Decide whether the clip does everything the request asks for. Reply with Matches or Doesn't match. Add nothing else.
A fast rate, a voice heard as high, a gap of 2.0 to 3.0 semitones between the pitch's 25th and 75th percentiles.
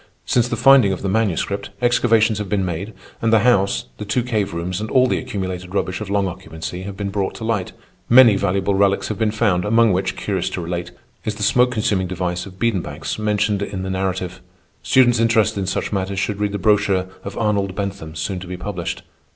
Doesn't match